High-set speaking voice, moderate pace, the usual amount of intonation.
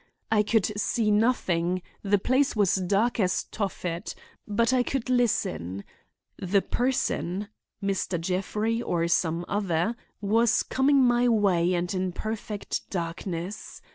No: high, 200 Hz; slow, 115 wpm; average, 4.2 semitones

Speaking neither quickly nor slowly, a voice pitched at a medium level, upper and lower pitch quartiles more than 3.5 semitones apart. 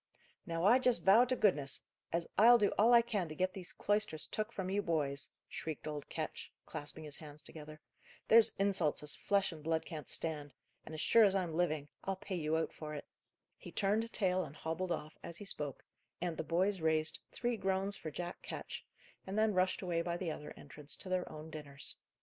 No: fast, 210 wpm; medium, 170 Hz; average, 4.3 semitones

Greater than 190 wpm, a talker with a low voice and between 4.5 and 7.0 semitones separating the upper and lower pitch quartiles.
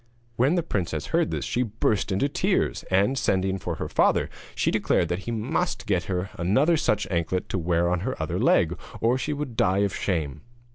Yes: fast, 205 wpm; low, 100 Hz; wide, 5.4 semitones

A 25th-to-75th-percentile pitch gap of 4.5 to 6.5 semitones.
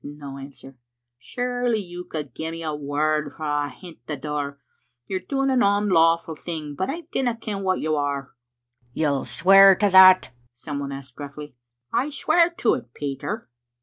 Yes: wide, 5.6 semitones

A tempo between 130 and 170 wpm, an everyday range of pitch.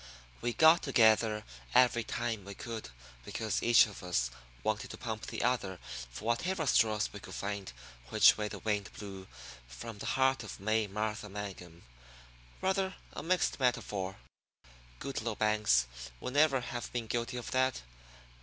Yes: average, 155 wpm; average, 3.4 semitones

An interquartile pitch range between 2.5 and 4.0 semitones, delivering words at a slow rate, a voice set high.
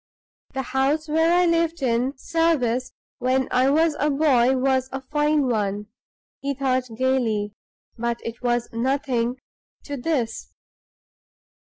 Yes: average, 3.5 semitones; slow, 130 wpm; very high, 265 Hz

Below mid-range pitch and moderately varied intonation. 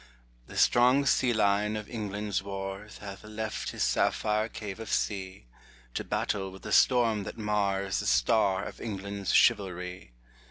No: low, 105 Hz; narrow, 1.9 semitones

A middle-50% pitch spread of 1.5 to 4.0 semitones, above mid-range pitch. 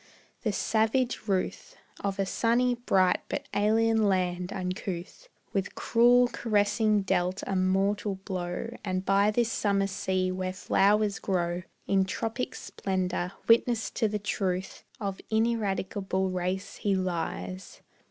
Yes: average, 2.8 semitones; high, 195 Hz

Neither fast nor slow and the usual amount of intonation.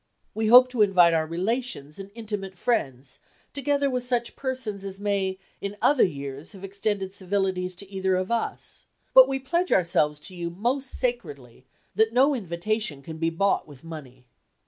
No: average, 170 wpm; wide, 5.8 semitones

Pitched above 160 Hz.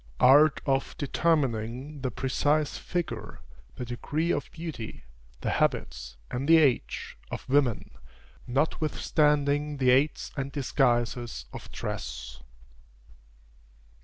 No: low, 135 Hz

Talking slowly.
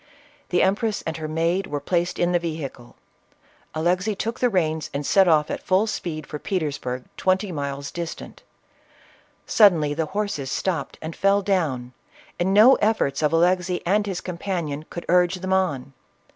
No: average, 160 wpm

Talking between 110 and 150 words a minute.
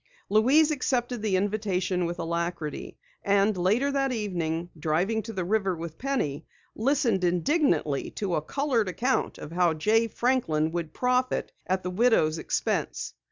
Yes: average, 145 wpm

